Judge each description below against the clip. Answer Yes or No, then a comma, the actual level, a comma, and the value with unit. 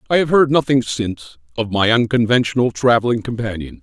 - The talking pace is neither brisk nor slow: Yes, average, 155 wpm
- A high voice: No, low, 120 Hz